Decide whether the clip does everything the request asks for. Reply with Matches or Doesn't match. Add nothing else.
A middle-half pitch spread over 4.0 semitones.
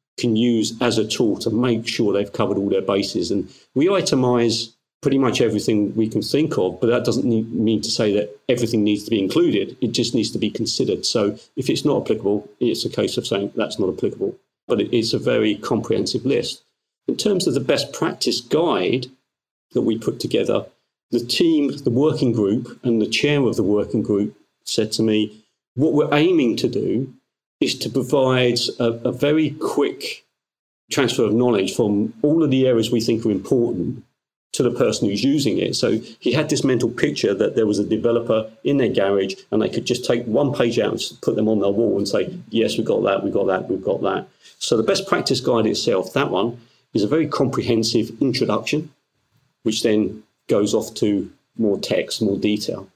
Doesn't match